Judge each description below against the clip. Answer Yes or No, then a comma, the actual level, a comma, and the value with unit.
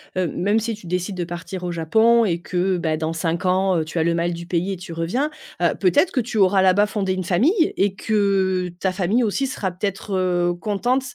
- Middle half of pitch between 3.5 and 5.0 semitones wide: No, average, 2.9 semitones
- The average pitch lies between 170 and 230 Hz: Yes, medium, 185 Hz